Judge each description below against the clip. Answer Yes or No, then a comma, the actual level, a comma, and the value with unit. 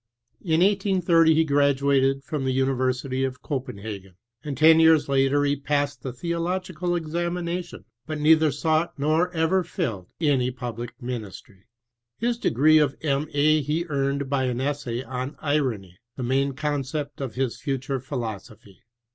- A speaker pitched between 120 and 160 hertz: Yes, medium, 140 Hz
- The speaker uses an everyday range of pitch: Yes, average, 3.7 semitones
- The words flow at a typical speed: Yes, average, 145 wpm